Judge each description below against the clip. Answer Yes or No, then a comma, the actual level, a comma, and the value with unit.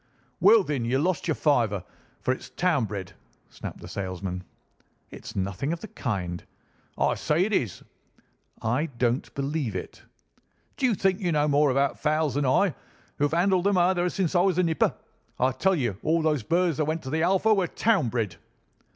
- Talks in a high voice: No, medium, 150 Hz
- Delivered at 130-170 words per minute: No, average, 185 wpm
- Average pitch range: No, wide, 6.6 semitones